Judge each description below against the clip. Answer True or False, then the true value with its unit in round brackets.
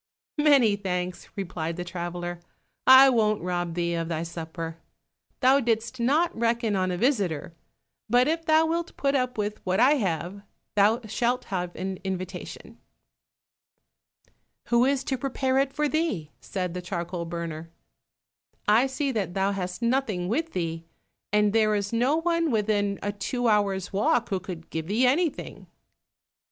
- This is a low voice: False (205 Hz)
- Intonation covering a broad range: True (6.3 semitones)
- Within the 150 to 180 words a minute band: True (155 wpm)